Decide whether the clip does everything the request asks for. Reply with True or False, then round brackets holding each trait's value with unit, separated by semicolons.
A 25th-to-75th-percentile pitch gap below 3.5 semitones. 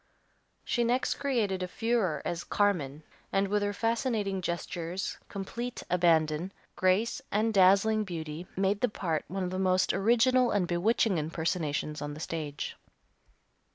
False (4.3 semitones)